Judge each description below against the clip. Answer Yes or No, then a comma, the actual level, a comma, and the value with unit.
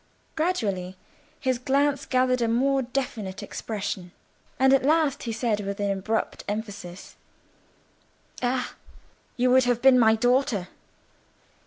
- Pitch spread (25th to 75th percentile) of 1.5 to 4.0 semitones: No, average, 4.4 semitones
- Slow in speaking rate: Yes, slow, 120 wpm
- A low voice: No, high, 245 Hz